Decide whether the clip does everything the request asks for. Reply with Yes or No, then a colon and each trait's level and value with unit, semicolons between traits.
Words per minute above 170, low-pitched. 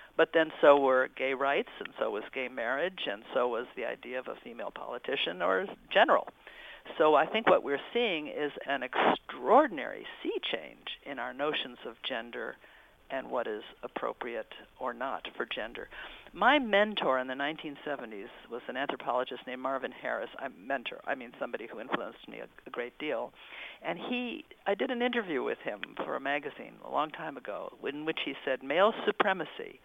No: average, 180 wpm; medium, 160 Hz